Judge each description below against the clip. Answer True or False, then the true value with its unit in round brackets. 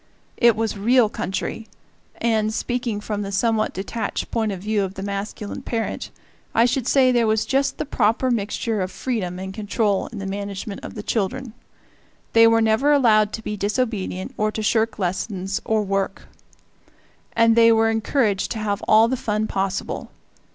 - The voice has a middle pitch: False (215 Hz)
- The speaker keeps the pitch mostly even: True (2.3 semitones)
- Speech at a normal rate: True (170 wpm)